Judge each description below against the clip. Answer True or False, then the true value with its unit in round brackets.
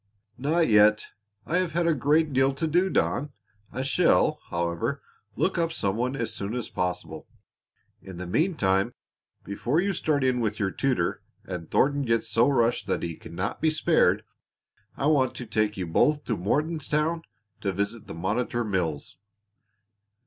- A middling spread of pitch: False (7.5 semitones)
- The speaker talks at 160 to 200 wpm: True (165 wpm)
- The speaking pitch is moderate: False (120 Hz)